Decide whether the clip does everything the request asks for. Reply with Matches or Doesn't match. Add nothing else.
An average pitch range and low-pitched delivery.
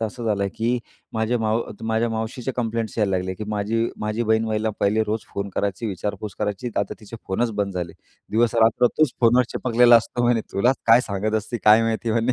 Doesn't match